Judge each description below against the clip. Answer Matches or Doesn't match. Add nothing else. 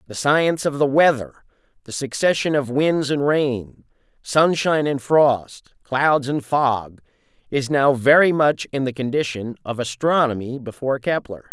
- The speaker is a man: Matches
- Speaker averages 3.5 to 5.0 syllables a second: Matches